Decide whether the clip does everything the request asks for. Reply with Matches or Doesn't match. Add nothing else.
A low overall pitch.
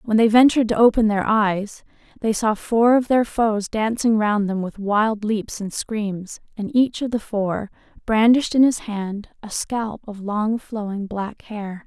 Doesn't match